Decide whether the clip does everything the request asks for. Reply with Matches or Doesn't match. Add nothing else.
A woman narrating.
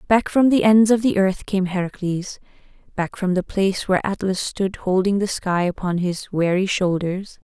Matches